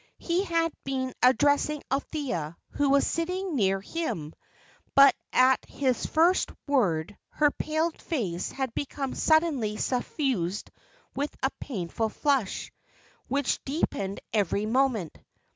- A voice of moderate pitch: No, very high, 270 Hz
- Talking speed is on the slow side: Yes, slow, 115 wpm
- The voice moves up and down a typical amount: No, wide, 6.2 semitones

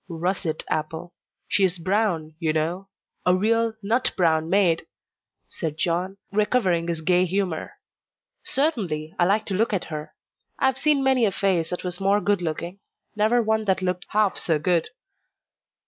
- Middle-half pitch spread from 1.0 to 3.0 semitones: No, average, 3.9 semitones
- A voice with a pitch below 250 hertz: Yes, medium, 185 Hz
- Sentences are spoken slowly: No, average, 165 wpm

